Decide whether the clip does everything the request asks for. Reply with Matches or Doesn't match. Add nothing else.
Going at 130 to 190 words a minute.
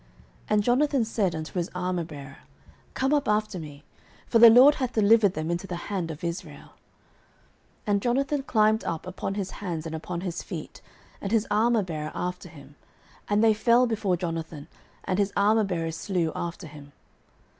Matches